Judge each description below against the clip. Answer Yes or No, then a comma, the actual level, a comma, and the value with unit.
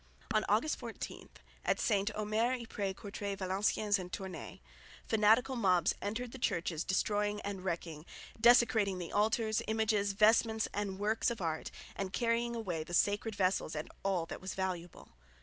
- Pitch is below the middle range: No, high, 205 Hz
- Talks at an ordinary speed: Yes, average, 150 wpm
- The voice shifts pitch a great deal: No, average, 2.9 semitones